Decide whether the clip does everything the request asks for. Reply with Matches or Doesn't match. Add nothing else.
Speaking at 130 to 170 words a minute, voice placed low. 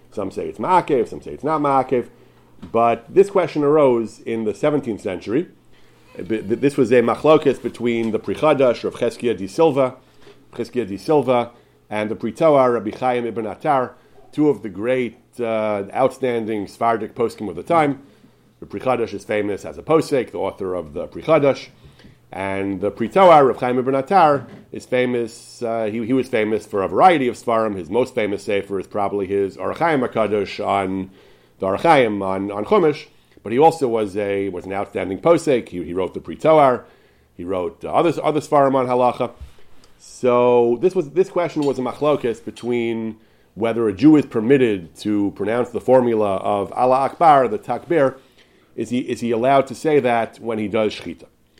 Doesn't match